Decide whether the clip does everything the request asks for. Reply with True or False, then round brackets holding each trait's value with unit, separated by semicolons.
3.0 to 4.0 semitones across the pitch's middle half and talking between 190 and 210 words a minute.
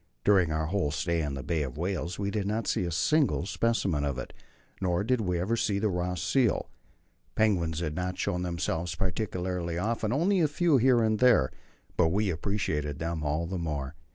False (4.8 semitones; 195 wpm)